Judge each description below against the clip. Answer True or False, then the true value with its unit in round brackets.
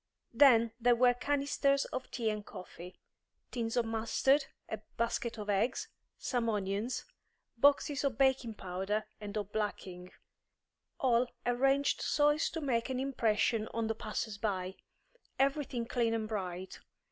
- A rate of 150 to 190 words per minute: False (140 wpm)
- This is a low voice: False (230 Hz)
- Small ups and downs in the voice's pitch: False (3.9 semitones)